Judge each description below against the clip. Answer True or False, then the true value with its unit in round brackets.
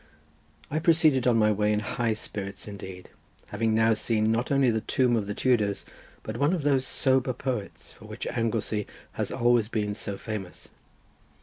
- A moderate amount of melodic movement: True (3.4 semitones)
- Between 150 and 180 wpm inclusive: True (175 wpm)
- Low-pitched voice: True (115 Hz)